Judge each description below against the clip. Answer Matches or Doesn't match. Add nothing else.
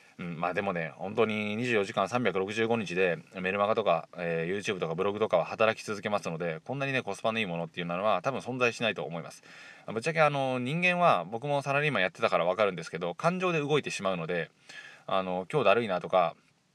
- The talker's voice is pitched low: Matches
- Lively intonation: Matches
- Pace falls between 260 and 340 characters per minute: Doesn't match